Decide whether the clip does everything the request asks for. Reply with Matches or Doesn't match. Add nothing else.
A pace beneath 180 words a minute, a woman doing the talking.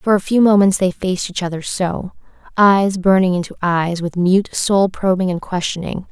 Doesn't match